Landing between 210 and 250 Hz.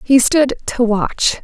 Yes: high, 245 Hz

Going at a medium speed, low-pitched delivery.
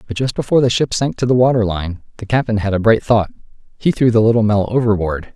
No: fast, 245 wpm; low, 115 Hz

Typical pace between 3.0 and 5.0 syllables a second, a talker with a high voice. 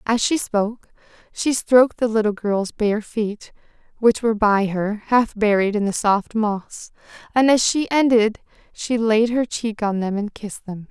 Yes: 4.3 syllables/s; high, 220 Hz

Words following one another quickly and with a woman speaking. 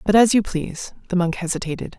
Yes: fast, 210 wpm; female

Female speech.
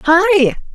Yes: female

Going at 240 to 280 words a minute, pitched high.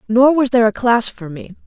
Yes: fast, 250 wpm; high, 235 Hz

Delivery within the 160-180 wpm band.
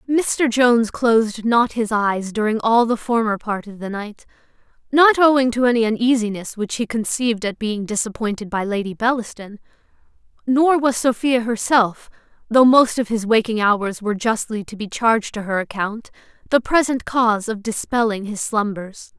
Yes: average, 165 wpm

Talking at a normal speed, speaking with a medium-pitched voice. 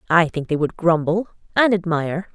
Yes: average, 180 wpm; medium, 175 Hz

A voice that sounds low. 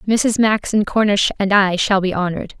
No: high, 200 Hz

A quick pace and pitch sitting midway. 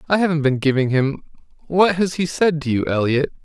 Yes: fast, 210 wpm; medium, 150 Hz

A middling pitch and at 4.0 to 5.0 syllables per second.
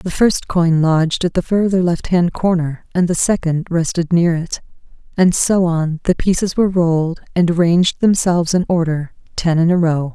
Yes: medium, 170 Hz; 4.9 syllables/s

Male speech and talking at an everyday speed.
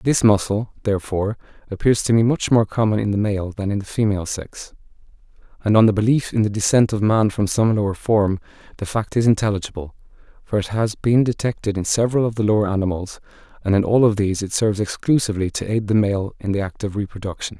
No: male; fast, 210 wpm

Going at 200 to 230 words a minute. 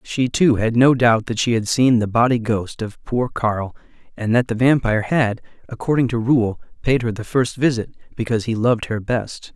Yes: fast, 205 wpm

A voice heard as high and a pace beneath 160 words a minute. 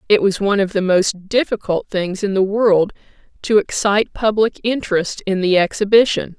No: high, 200 Hz; average, 170 wpm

